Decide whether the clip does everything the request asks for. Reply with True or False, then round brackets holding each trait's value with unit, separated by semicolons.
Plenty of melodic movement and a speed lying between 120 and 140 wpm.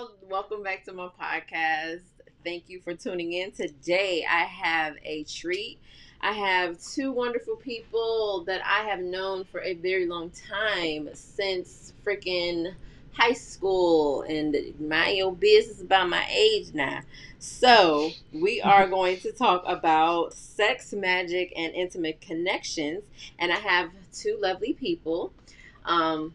False (3.4 semitones; 135 wpm)